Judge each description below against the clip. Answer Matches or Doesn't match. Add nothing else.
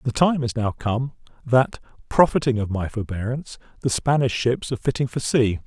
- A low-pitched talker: Matches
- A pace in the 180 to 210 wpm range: Doesn't match